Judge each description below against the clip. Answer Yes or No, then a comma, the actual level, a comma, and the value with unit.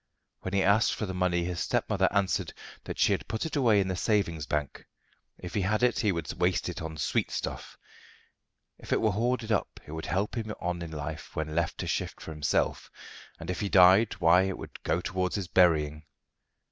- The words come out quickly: Yes, fast, 210 wpm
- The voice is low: Yes, very low, 90 Hz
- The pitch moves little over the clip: No, average, 3.8 semitones